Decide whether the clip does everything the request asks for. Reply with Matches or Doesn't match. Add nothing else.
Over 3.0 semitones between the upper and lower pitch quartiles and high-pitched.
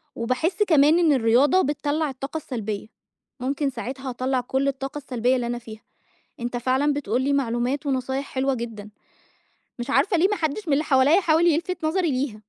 Matches